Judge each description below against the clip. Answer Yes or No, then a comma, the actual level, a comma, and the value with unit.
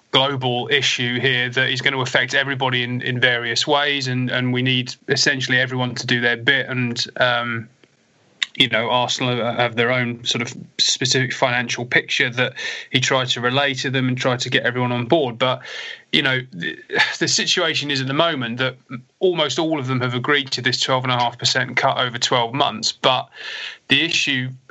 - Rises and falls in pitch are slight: Yes, narrow, 1.6 semitones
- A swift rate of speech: No, average, 185 wpm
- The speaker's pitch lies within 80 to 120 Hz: No, low, 130 Hz